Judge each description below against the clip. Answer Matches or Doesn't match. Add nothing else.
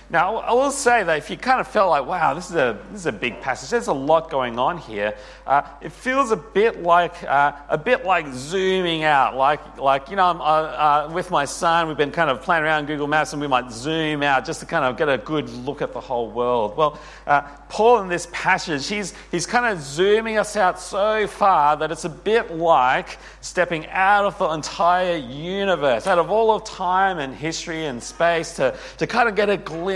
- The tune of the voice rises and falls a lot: Doesn't match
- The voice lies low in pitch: Doesn't match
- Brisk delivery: Matches